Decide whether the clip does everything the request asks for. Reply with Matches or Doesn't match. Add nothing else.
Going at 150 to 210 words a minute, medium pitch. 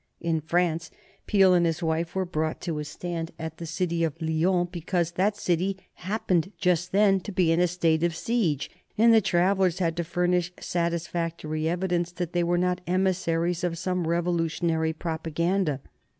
Matches